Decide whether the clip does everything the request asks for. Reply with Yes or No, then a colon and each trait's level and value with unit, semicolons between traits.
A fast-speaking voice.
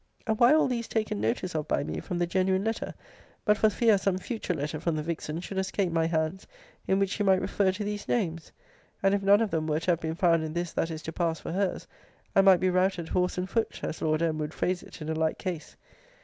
Yes: fast, 260 wpm